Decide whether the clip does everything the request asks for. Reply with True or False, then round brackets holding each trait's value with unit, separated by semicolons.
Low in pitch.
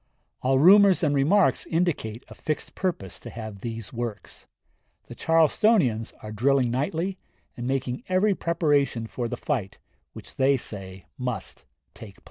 True (130 Hz)